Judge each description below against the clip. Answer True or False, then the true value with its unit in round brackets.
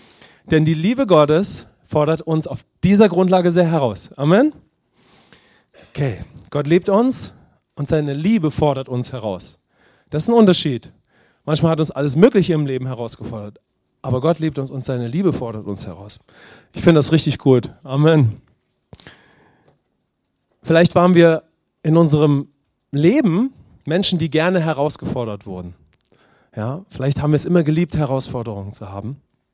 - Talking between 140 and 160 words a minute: True (145 wpm)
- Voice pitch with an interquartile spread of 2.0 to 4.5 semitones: False (5.1 semitones)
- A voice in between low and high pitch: True (150 Hz)